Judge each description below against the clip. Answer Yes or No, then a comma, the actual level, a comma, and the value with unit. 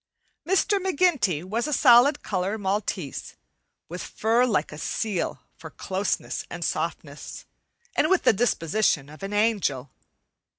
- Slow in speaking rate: Yes, slow, 130 wpm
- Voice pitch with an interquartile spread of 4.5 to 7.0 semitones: Yes, wide, 5.4 semitones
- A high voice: Yes, high, 205 Hz